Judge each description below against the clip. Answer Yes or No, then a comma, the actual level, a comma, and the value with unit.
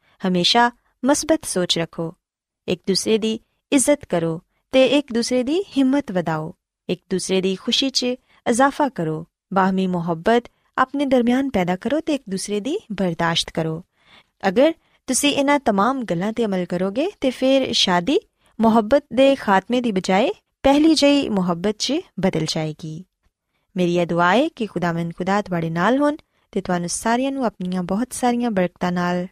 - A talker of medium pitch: No, high, 210 Hz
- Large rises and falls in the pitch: Yes, wide, 6.8 semitones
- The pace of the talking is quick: No, average, 150 wpm